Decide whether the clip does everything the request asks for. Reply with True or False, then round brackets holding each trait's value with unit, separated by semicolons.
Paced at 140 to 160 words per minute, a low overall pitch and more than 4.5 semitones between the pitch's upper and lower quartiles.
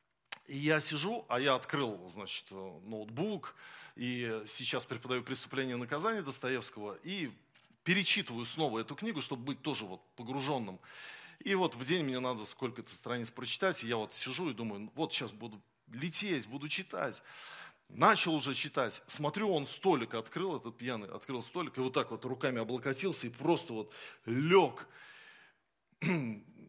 True (150 wpm; 130 Hz; 5.0 semitones)